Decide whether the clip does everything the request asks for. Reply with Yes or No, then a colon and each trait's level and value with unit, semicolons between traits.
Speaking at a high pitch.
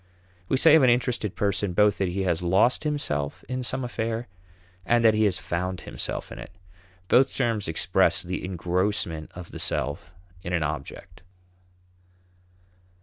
No: low, 100 Hz